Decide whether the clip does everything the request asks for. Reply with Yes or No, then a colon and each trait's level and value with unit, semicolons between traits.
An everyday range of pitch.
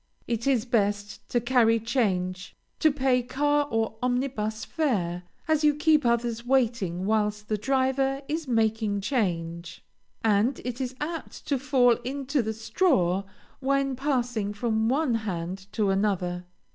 Yes: average, 4.5 semitones